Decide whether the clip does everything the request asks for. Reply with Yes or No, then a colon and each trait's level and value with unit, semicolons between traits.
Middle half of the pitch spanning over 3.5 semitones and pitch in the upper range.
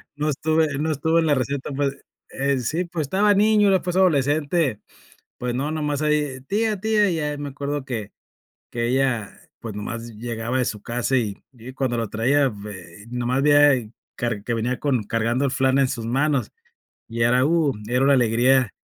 No: average, 4.0 semitones; low, 135 Hz